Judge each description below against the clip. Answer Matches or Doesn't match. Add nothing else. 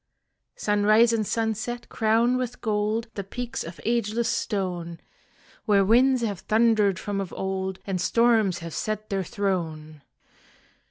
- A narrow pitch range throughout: Doesn't match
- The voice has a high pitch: Matches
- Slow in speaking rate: Matches